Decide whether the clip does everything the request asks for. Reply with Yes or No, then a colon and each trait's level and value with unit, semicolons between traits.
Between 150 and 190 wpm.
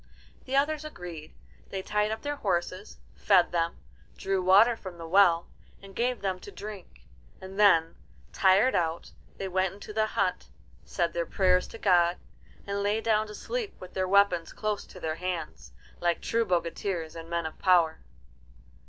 Yes: average, 170 wpm